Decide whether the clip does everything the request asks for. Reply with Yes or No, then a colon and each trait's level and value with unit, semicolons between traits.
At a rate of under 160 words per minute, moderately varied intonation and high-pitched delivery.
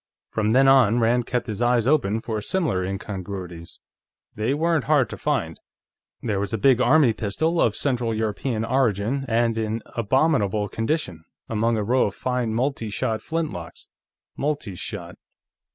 No: average, 150 wpm; average, 4.3 semitones; low, 115 Hz